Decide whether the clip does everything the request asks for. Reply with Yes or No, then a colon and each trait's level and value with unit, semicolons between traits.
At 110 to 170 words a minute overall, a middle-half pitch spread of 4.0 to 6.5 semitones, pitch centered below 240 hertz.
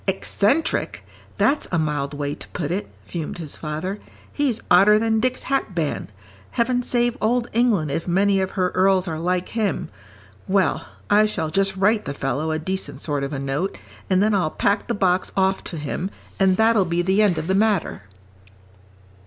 No: average, 180 wpm; average, 4.6 semitones; high, 190 Hz